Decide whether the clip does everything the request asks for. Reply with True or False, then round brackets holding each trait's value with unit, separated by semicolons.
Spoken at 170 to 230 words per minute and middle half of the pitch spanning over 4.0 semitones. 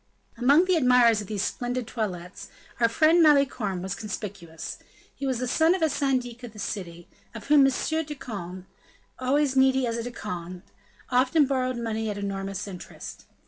True (175 wpm; 5.2 semitones)